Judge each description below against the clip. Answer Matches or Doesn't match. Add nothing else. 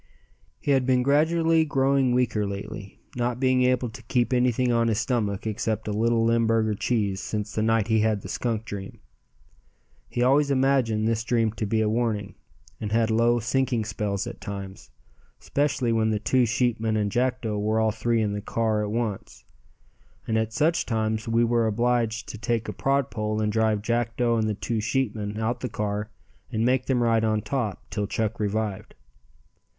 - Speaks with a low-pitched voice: Matches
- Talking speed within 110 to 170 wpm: Doesn't match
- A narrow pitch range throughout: Matches